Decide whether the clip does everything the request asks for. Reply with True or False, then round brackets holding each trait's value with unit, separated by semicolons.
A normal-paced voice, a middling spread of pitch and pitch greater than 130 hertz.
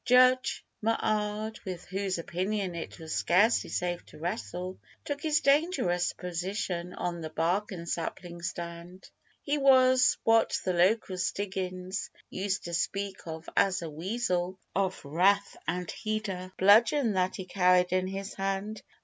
True (145 wpm; 3.4 semitones; 185 Hz)